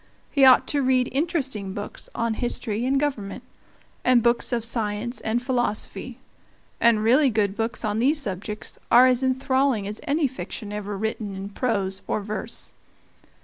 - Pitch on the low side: No, high, 235 Hz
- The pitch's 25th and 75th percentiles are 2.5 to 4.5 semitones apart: Yes, average, 3.8 semitones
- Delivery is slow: No, average, 155 wpm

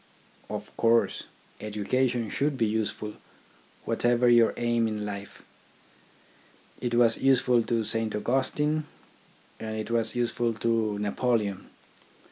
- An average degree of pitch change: No, narrow, 2.1 semitones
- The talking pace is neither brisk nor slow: No, slow, 110 wpm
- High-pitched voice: No, low, 115 Hz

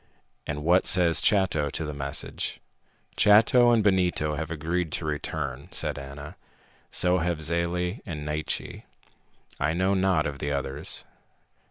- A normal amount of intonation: Yes, average, 3.6 semitones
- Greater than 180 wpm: No, average, 140 wpm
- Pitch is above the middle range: No, very low, 80 Hz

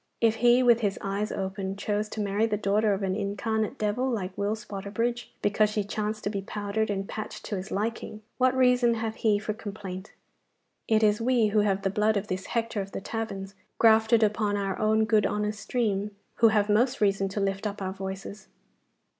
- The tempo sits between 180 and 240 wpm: Yes, average, 200 wpm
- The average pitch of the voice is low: No, high, 210 Hz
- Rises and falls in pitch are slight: Yes, narrow, 1.9 semitones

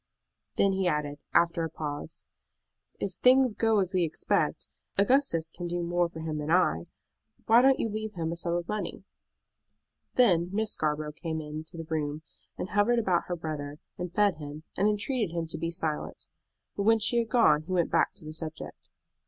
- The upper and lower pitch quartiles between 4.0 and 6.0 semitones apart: Yes, average, 4.7 semitones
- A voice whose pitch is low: No, medium, 170 Hz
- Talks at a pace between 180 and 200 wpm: Yes, average, 190 wpm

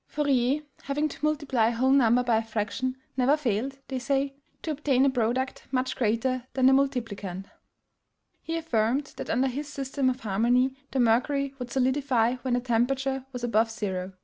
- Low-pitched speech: No, very high, 255 Hz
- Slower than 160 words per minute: No, average, 175 wpm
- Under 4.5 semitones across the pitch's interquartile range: Yes, average, 2.8 semitones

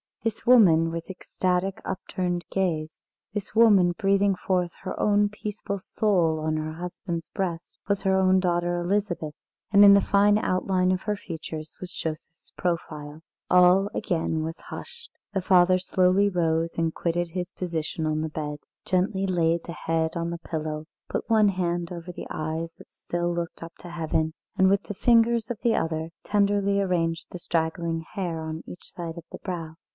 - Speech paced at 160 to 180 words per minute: Yes, average, 170 wpm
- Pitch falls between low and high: Yes, medium, 175 Hz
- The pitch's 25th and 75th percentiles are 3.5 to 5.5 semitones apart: No, average, 2.9 semitones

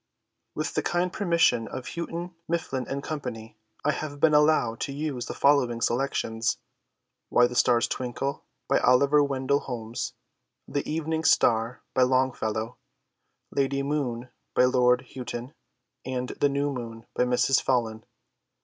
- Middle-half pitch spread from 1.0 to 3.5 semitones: Yes, average, 3.0 semitones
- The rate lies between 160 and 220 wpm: No, average, 140 wpm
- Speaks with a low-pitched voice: Yes, low, 130 Hz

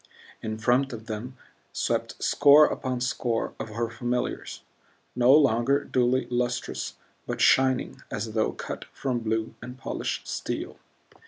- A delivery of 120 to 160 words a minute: Yes, slow, 135 wpm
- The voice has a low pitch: Yes, low, 120 Hz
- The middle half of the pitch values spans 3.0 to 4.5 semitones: No, narrow, 2.4 semitones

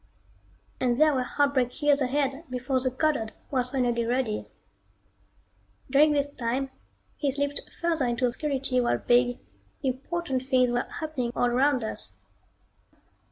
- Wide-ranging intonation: No, narrow, 2.6 semitones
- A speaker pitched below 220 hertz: No, very high, 260 Hz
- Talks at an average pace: No, slow, 130 wpm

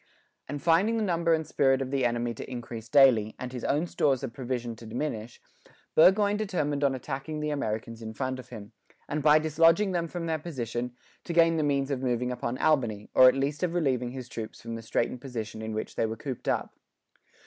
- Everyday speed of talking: No, fast, 215 wpm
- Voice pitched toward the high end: No, low, 135 Hz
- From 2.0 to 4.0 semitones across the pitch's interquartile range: No, average, 4.7 semitones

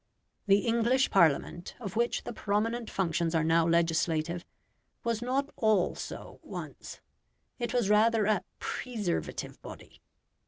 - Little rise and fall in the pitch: No, wide, 5.5 semitones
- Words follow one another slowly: Yes, slow, 125 wpm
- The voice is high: Yes, high, 210 Hz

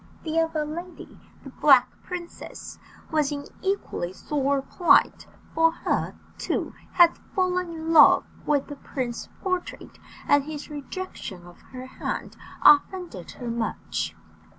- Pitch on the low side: No, very high, 300 Hz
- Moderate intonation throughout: Yes, average, 4.1 semitones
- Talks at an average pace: No, slow, 130 wpm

